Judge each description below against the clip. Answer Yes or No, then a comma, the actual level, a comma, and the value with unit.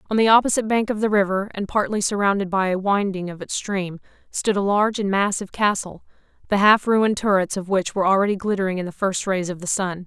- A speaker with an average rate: No, fast, 225 wpm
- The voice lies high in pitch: Yes, high, 195 Hz